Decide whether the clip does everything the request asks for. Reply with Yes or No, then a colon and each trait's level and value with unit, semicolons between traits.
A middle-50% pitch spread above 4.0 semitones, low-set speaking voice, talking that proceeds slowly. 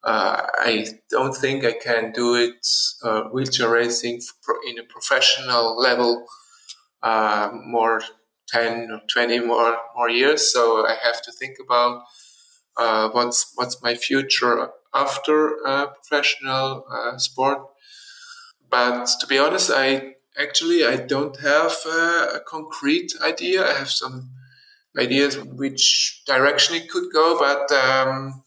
Yes: average, 4.6 semitones; low, 130 Hz; slow, 130 wpm